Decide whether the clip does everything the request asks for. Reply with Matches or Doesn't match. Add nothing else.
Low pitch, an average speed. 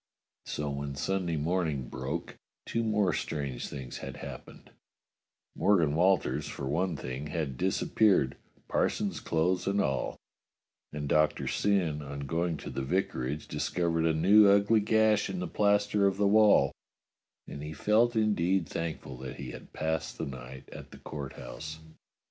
Matches